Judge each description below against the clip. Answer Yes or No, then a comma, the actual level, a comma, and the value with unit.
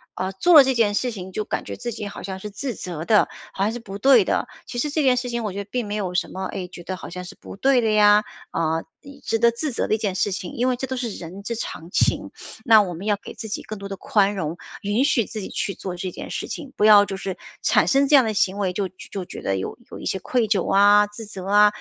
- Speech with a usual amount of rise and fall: Yes, average, 3.6 semitones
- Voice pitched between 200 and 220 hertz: Yes, high, 205 Hz